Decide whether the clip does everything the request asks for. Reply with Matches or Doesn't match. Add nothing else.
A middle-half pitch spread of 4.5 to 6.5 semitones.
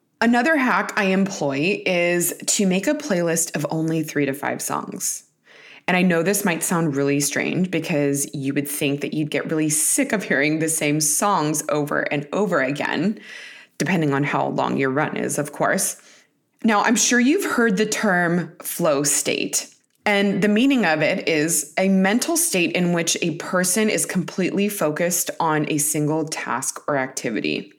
Matches